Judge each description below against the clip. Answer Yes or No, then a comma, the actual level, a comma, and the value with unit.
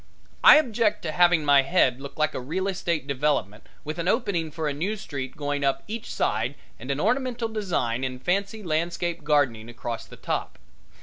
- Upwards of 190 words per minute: No, average, 185 wpm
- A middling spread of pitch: No, wide, 5.7 semitones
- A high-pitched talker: No, medium, 155 Hz